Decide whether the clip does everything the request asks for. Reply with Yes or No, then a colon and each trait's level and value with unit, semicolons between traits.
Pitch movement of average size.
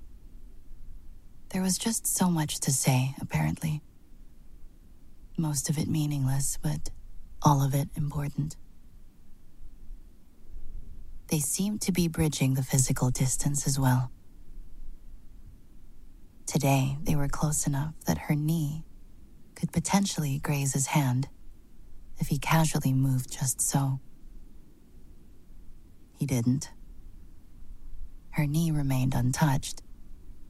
No: wide, 8.4 semitones